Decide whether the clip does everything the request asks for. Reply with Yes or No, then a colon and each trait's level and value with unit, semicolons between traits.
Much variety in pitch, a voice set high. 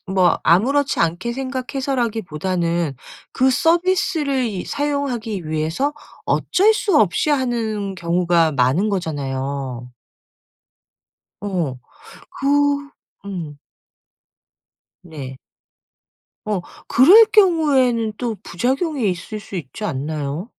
Yes: wide, 8.5 semitones; high, 210 Hz